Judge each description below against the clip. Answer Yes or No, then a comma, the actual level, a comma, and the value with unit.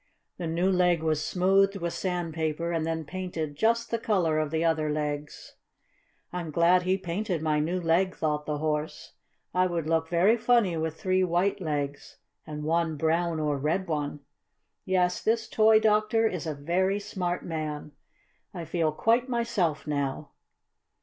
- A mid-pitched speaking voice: Yes, medium, 170 Hz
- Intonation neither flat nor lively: Yes, average, 3.3 semitones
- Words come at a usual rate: Yes, average, 160 wpm